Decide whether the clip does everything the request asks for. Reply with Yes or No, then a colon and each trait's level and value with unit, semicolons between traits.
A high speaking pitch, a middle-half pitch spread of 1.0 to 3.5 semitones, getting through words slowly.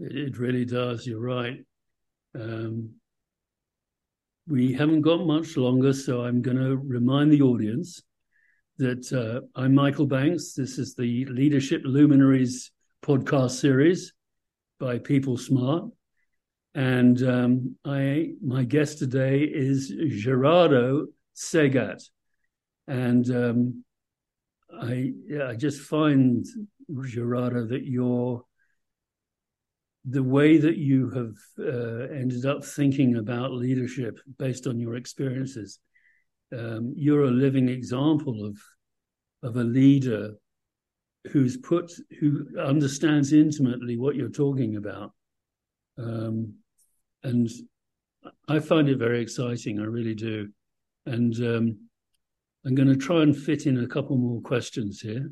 No: low, 130 Hz; average, 2.7 semitones; slow, 120 wpm